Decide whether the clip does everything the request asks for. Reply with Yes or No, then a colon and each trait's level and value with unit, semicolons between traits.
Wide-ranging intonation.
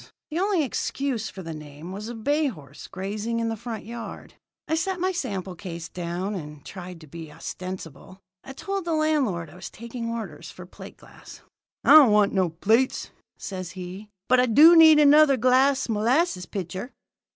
Yes: wide, 7.1 semitones